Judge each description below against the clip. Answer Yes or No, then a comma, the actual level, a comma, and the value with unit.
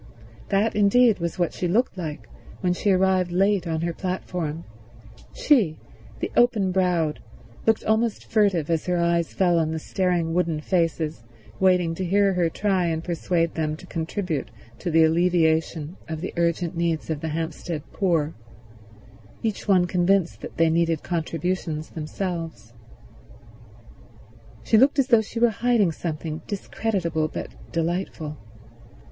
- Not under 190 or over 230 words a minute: No, average, 145 wpm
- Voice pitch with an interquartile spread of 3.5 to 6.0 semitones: No, average, 2.9 semitones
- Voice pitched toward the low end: No, medium, 175 Hz